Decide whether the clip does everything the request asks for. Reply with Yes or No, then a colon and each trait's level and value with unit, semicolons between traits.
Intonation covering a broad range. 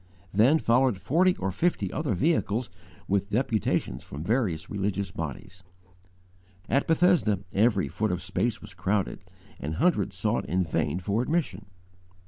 Yes: wide, 5.9 semitones